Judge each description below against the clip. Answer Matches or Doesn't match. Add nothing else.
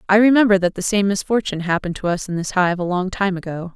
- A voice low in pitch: Doesn't match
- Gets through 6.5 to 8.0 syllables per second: Matches